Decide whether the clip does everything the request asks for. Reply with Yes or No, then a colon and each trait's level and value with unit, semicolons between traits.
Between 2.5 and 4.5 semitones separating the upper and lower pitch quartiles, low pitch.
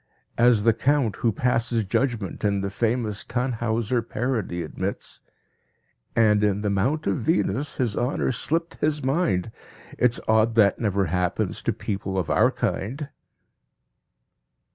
Yes: average, 3.9 semitones; low, 115 Hz